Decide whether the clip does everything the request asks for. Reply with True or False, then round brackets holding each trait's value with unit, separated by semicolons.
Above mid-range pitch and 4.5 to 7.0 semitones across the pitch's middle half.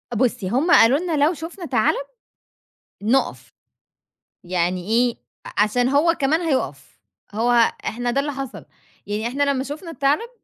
True (265 Hz; 5.0 semitones)